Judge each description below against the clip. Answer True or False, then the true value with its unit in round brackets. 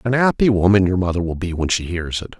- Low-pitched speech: True (95 Hz)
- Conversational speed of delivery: False (275 wpm)